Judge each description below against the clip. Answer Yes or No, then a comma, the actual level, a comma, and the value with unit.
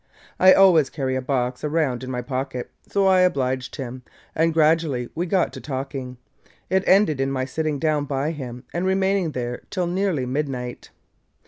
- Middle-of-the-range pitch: Yes, medium, 145 Hz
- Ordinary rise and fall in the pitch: Yes, average, 4.8 semitones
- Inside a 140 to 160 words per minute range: No, average, 175 wpm